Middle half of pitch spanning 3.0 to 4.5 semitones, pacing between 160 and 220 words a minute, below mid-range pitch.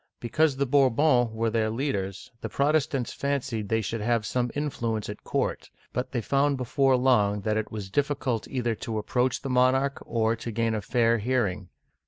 Yes: average, 3.5 semitones; average, 180 wpm; low, 120 Hz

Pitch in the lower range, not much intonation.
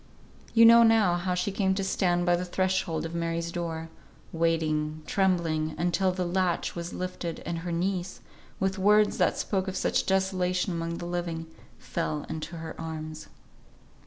No: medium, 175 Hz; narrow, 2.3 semitones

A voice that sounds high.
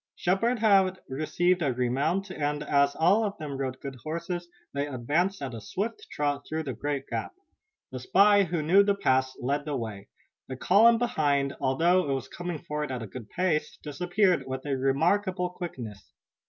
No: medium, 150 Hz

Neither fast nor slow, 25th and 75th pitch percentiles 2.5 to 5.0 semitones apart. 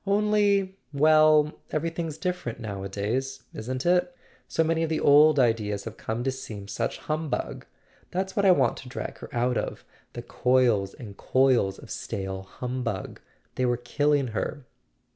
No: average, 155 wpm; wide, 5.5 semitones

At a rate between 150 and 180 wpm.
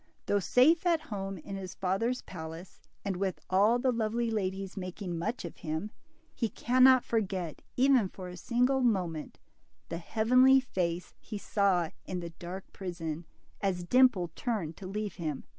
Yes: average, 160 wpm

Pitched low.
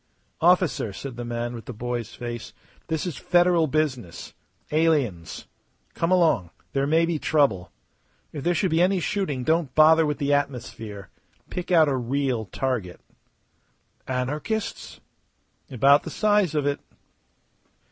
No: medium, 145 Hz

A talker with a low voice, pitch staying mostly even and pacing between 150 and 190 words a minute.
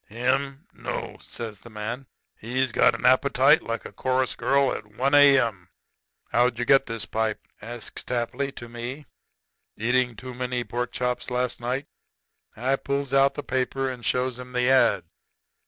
Yes: low, 125 Hz; narrow, 2.2 semitones; average, 160 wpm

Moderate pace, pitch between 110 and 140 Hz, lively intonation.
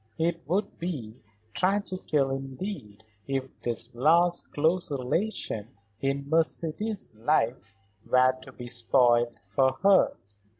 No: slow, 110 wpm; low, 135 Hz; wide, 6.0 semitones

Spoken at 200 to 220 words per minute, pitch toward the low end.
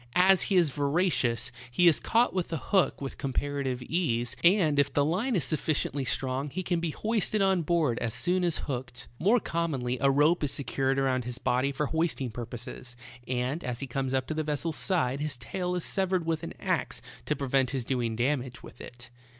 No: fast, 205 wpm; medium, 145 Hz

